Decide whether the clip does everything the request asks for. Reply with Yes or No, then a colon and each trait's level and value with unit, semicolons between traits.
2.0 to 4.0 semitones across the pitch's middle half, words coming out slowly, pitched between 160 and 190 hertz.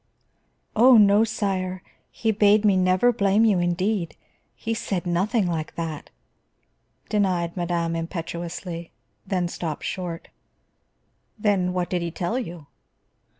Yes: average, 3.2 semitones; slow, 120 wpm; medium, 185 Hz